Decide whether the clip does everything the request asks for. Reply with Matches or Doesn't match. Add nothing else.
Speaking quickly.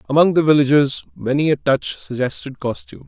Doesn't match